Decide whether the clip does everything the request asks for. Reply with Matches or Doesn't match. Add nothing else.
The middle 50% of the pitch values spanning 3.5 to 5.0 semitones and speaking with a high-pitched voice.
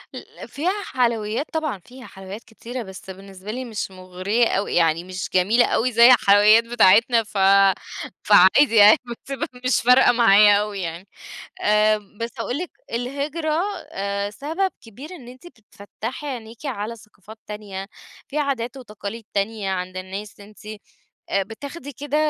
Matches